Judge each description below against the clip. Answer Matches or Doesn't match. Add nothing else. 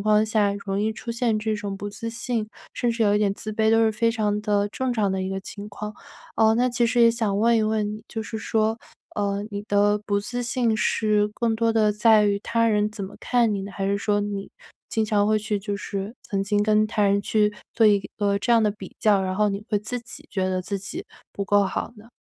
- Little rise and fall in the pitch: Matches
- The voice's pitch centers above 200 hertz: Matches